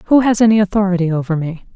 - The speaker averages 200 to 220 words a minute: Yes, fast, 205 wpm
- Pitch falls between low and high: No, high, 195 Hz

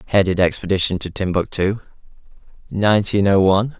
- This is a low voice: Yes, low, 100 Hz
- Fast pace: No, slow, 110 wpm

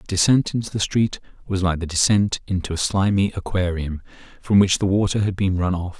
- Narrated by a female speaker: No, male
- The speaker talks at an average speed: No, fast, 210 wpm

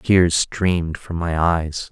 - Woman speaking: No, male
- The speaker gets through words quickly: No, average, 155 wpm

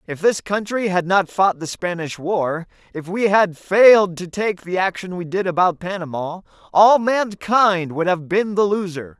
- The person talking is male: Yes, male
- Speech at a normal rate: Yes, average, 185 wpm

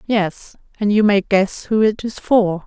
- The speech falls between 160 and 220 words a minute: Yes, fast, 205 wpm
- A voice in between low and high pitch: No, high, 205 Hz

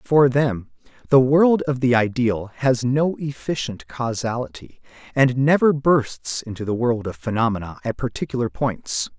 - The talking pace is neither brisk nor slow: Yes, average, 145 wpm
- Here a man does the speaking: Yes, male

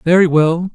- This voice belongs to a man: Yes, male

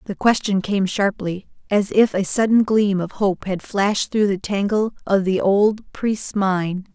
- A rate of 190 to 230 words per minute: No, average, 180 wpm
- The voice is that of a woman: Yes, female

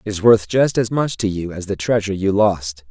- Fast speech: Yes, fast, 270 wpm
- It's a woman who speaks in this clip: No, male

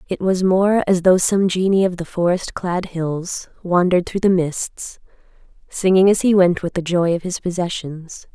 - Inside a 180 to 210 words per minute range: Yes, average, 185 wpm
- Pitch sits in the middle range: Yes, medium, 180 Hz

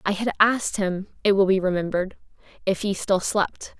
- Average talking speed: Yes, average, 190 wpm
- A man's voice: No, female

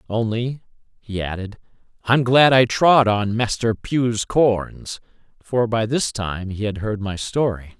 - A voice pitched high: No, low, 115 Hz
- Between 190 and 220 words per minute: No, average, 155 wpm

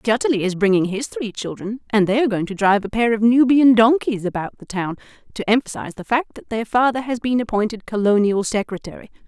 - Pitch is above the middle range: Yes, high, 220 Hz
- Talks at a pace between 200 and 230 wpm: Yes, fast, 205 wpm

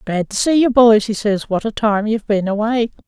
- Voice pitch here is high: Yes, high, 215 Hz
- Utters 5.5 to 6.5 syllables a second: No, 5.3 syllables/s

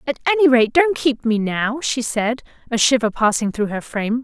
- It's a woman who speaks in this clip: Yes, female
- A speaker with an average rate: No, fast, 215 wpm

